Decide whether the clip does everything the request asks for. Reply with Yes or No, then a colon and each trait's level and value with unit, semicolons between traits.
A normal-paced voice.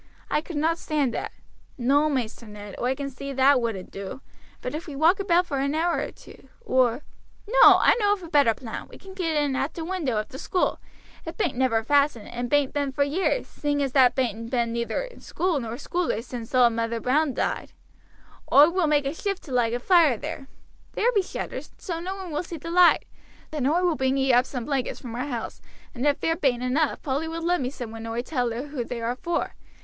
No: fast, 230 wpm